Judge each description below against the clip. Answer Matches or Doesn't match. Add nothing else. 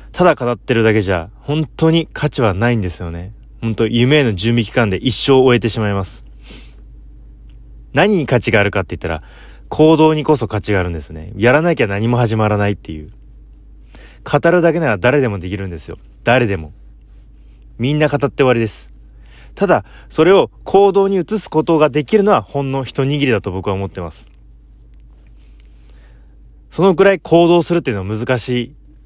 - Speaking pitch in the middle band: Doesn't match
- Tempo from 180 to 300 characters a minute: Doesn't match